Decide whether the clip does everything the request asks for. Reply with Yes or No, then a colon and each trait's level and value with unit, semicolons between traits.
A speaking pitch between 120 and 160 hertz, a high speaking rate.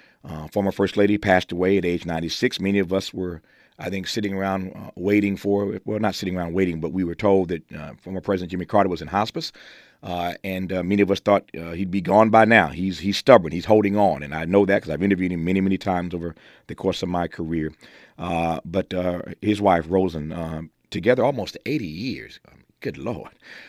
No: very low, 95 Hz; fast, 225 wpm